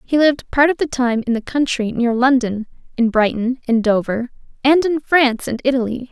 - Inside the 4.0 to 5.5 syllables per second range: Yes, 5.3 syllables/s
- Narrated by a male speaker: No, female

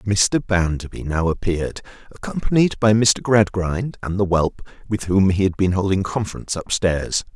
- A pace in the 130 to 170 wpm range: Yes, average, 165 wpm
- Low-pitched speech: Yes, very low, 95 Hz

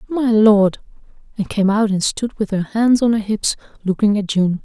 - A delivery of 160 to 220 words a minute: Yes, fast, 205 wpm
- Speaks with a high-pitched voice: Yes, high, 210 Hz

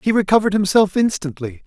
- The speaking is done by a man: Yes, male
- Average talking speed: Yes, average, 145 wpm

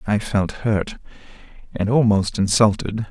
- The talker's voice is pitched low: Yes, low, 105 Hz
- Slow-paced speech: Yes, slow, 115 wpm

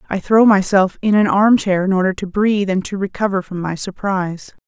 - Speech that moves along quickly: Yes, fast, 220 wpm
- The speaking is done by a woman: Yes, female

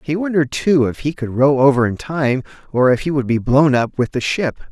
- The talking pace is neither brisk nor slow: No, fast, 255 wpm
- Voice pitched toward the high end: No, medium, 140 Hz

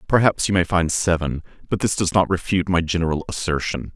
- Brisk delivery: No, average, 195 wpm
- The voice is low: Yes, very low, 90 Hz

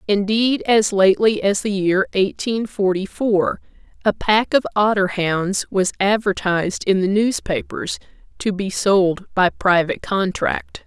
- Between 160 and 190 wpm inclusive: No, average, 140 wpm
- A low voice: No, high, 200 Hz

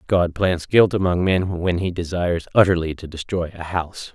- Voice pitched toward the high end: No, very low, 90 Hz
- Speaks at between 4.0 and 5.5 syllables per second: Yes, 5.1 syllables/s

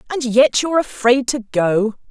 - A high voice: Yes, very high, 250 Hz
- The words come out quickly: No, average, 170 wpm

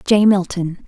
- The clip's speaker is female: Yes, female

